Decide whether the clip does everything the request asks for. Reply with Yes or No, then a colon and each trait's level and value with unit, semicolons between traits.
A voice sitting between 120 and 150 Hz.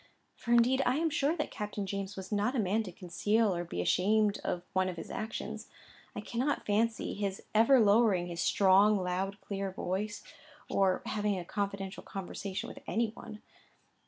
No: high, 205 Hz